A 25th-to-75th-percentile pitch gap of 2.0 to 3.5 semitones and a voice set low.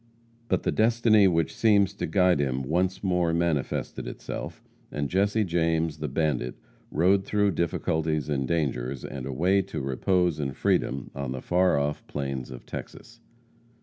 No: wide, 5.5 semitones; very low, 80 Hz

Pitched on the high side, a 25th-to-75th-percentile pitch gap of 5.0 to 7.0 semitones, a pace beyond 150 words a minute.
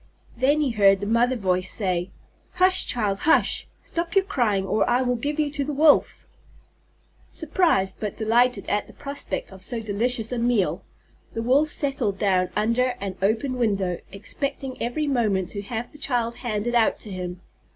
Yes: high, 235 Hz; average, 5.3 semitones; average, 170 wpm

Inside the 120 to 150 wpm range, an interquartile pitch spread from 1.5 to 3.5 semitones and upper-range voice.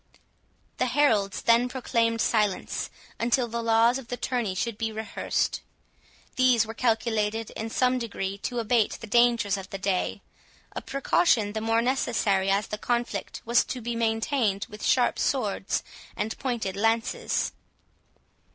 Yes: average, 145 wpm; narrow, 2.4 semitones; high, 230 Hz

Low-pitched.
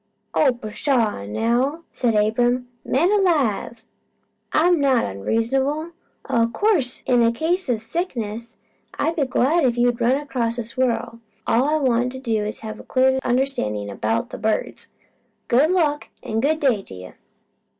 No: high, 245 Hz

